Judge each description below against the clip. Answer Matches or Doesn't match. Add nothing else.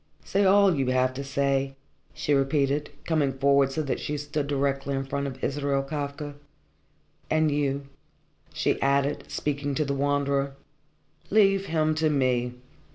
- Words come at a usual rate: Matches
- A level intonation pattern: Matches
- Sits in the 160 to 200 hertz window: Doesn't match